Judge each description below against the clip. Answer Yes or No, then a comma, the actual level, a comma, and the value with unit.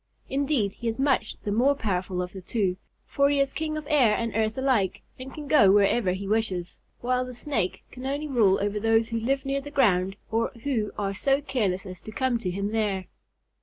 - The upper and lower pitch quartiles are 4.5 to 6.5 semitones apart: Yes, average, 5.3 semitones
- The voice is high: Yes, high, 225 Hz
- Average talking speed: No, fast, 215 wpm